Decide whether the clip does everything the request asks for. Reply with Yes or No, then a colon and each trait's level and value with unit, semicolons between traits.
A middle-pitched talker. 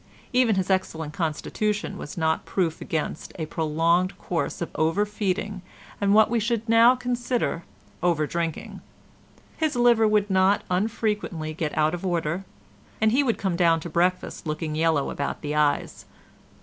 Yes: medium, 180 Hz